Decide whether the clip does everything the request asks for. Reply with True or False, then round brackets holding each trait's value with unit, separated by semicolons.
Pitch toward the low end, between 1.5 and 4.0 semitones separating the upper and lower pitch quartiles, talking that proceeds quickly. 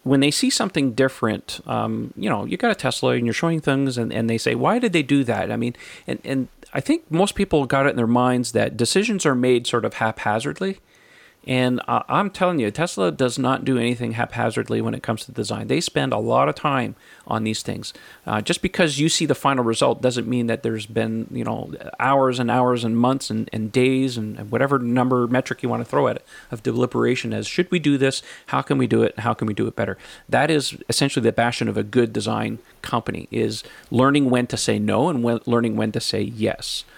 True (125 Hz; 3.2 semitones; 235 wpm)